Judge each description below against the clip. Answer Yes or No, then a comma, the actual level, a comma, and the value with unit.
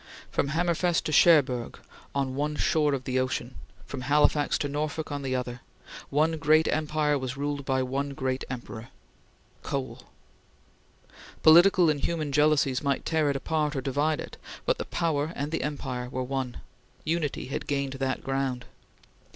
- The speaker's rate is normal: Yes, average, 160 wpm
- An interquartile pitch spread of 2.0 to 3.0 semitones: Yes, average, 2.7 semitones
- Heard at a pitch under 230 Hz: Yes, medium, 140 Hz